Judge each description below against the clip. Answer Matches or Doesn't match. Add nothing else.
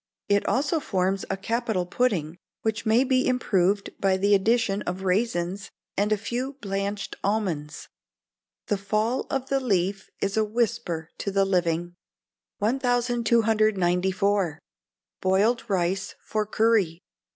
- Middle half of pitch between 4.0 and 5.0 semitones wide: Doesn't match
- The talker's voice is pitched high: Matches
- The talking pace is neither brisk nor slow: Doesn't match